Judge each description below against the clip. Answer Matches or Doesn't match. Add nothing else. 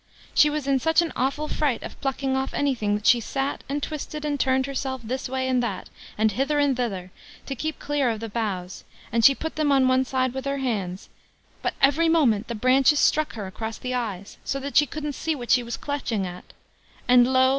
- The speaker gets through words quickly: Matches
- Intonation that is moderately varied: Matches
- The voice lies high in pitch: Matches